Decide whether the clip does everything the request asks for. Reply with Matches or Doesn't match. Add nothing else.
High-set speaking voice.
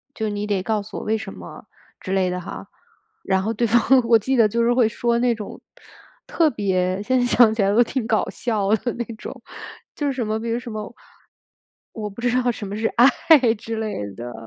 Matches